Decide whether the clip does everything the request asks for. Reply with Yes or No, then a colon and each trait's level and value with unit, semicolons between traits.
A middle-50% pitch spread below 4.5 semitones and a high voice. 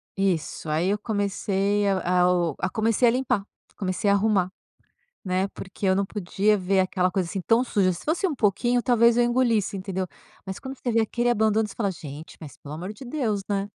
Yes: average, 3.6 semitones; high, 200 Hz